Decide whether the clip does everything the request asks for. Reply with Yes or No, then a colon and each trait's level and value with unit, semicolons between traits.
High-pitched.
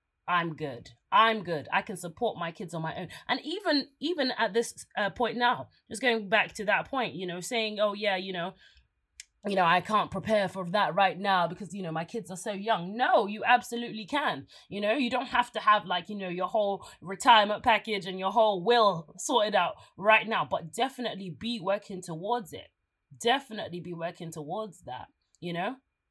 Yes: high, 205 Hz